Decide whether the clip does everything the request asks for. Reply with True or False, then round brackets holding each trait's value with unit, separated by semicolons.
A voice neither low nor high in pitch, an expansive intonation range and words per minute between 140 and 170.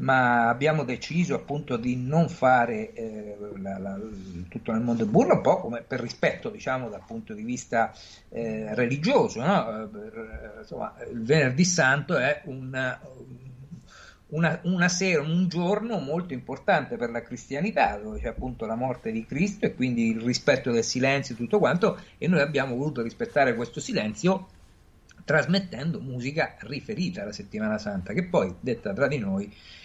False (130 Hz; 7.5 semitones; 155 wpm)